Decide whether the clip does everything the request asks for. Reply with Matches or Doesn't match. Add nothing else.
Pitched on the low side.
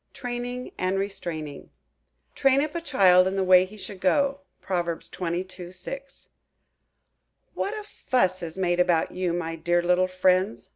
Doesn't match